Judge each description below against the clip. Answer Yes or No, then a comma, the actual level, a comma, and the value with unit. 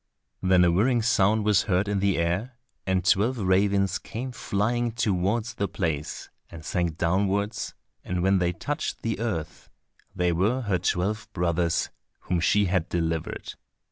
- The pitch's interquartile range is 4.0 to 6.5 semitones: No, average, 3.5 semitones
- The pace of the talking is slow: No, average, 150 wpm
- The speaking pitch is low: Yes, very low, 95 Hz